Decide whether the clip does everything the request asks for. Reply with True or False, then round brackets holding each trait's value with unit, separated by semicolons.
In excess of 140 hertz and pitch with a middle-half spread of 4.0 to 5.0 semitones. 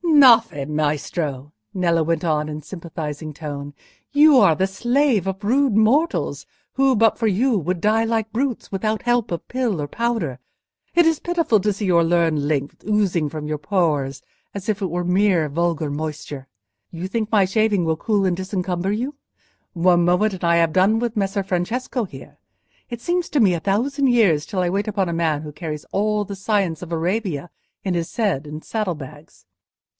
False (185 Hz; 5.5 semitones)